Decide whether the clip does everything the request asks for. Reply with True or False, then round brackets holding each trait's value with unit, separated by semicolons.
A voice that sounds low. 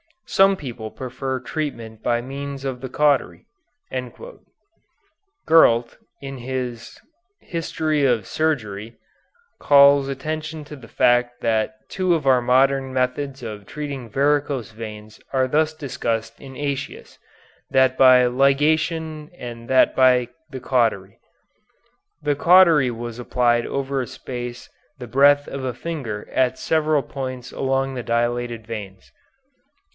True (130 Hz)